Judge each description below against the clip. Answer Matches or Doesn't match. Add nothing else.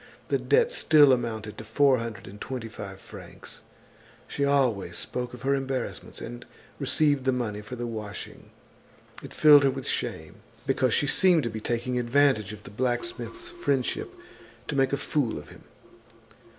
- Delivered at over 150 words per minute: Matches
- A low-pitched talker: Matches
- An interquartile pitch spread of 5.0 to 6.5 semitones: Doesn't match